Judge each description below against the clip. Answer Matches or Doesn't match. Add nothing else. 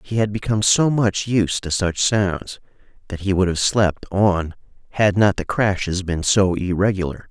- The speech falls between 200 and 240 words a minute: Doesn't match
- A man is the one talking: Matches